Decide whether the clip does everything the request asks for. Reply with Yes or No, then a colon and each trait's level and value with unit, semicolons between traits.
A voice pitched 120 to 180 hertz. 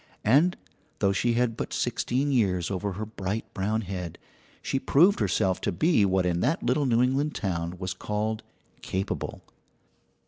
No: low, 105 Hz